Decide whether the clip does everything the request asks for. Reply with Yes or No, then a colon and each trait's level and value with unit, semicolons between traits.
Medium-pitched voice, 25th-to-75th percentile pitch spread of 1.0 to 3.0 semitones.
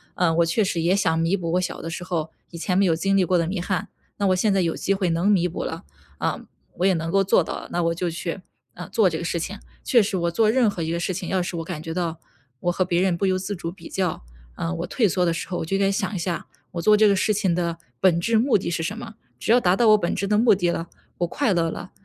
Yes: medium, 180 Hz; average, 2.7 semitones